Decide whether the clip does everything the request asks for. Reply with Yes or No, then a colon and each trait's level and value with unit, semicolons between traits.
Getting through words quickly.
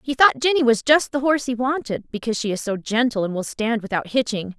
Yes: fast, 250 wpm